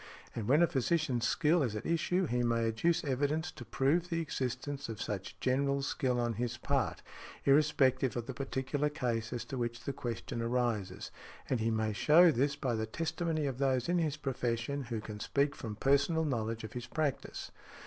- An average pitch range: Yes, average, 4.0 semitones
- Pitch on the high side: No, low, 130 Hz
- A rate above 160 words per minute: Yes, average, 190 wpm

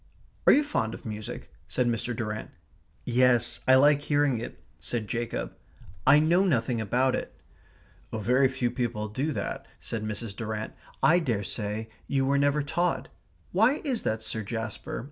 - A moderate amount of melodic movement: Yes, average, 4.3 semitones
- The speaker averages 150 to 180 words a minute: Yes, average, 155 wpm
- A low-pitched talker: Yes, low, 120 Hz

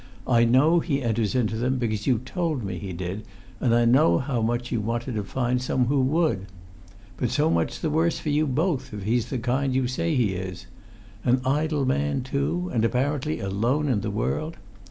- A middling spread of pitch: Yes, average, 4.3 semitones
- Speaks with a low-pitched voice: Yes, low, 125 Hz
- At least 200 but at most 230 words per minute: Yes, fast, 205 wpm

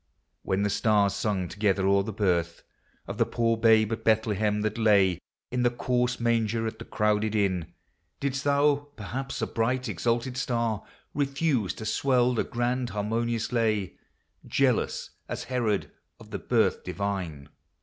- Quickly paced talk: No, average, 150 wpm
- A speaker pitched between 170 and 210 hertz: No, low, 110 Hz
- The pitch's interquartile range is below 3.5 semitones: Yes, average, 3.1 semitones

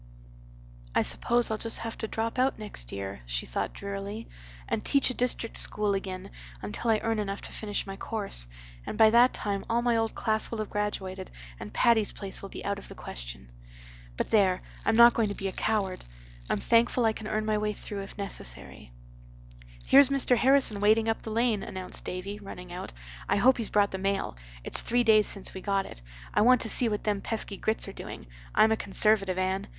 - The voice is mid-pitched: No, high, 210 Hz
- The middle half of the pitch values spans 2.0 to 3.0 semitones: Yes, narrow, 2.5 semitones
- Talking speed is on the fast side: Yes, fast, 210 wpm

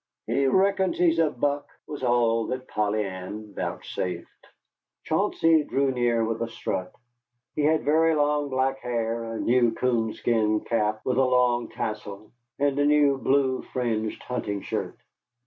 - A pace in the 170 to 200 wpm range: No, average, 145 wpm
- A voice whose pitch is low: Yes, low, 125 Hz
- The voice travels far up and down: No, average, 4.2 semitones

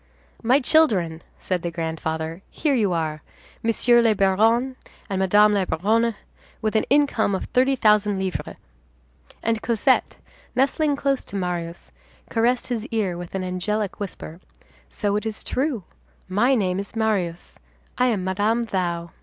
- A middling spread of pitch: Yes, average, 4.4 semitones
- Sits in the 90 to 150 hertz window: No, high, 210 Hz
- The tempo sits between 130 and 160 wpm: Yes, average, 145 wpm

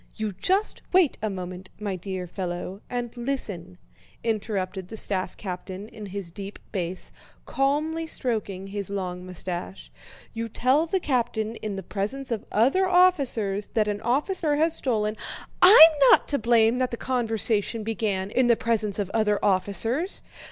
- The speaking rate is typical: Yes, average, 150 wpm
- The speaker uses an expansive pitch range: No, average, 4.7 semitones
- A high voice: Yes, high, 215 Hz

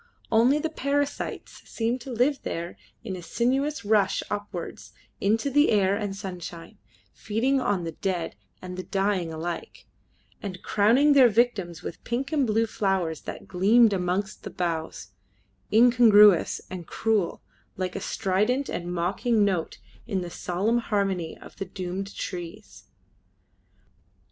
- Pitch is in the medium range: No, high, 200 Hz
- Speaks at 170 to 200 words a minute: No, average, 140 wpm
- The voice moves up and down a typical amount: Yes, average, 4.7 semitones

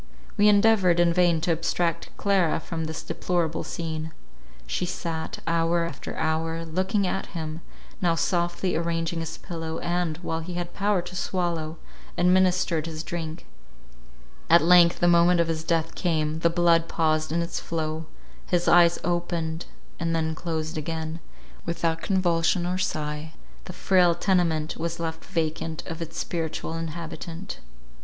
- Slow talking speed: No, average, 150 wpm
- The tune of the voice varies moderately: No, narrow, 1.5 semitones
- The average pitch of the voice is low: No, medium, 165 Hz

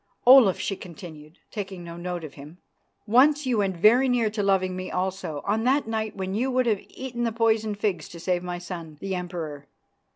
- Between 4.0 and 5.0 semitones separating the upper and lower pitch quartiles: Yes, average, 4.4 semitones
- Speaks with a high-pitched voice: Yes, high, 195 Hz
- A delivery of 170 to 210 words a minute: Yes, average, 200 wpm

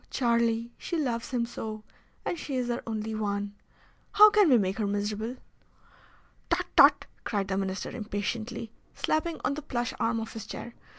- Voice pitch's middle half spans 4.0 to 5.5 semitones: No, average, 2.7 semitones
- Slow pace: No, average, 170 wpm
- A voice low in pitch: No, high, 230 Hz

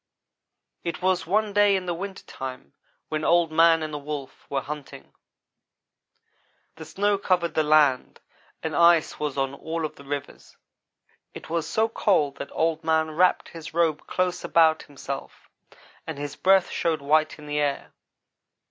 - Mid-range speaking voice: Yes, medium, 160 Hz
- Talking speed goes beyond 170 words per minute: No, average, 160 wpm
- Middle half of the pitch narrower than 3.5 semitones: Yes, average, 2.8 semitones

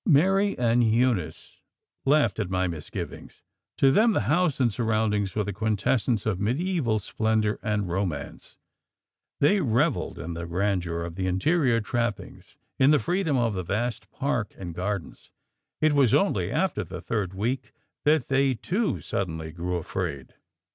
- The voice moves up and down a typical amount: No, wide, 6.5 semitones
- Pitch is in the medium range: No, low, 110 Hz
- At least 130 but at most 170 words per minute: Yes, average, 150 wpm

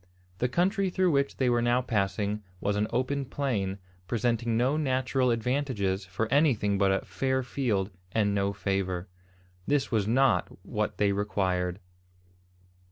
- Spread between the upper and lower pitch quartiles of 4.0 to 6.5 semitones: Yes, average, 4.8 semitones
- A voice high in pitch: No, low, 115 Hz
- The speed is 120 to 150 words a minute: Yes, average, 145 wpm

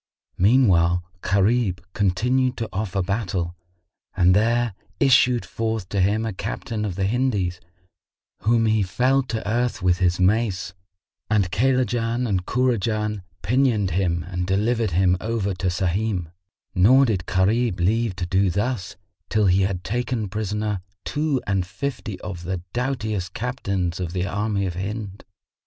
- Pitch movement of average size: Yes, average, 4.1 semitones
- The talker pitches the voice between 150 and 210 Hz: No, low, 105 Hz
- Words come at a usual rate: Yes, average, 145 wpm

